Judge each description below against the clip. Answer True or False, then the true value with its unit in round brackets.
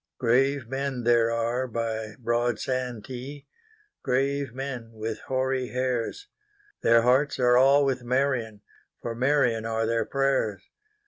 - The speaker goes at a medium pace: False (110 wpm)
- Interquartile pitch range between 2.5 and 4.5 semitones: True (2.9 semitones)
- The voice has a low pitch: True (125 Hz)